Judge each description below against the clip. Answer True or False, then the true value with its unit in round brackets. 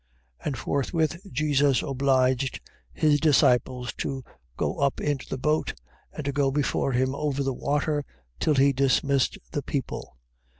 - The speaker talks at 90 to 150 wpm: True (145 wpm)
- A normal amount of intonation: False (1.8 semitones)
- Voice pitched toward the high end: False (140 Hz)